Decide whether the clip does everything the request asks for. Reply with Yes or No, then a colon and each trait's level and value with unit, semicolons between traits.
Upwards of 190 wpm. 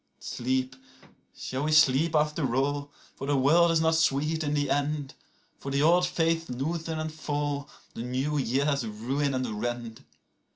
No: average, 155 wpm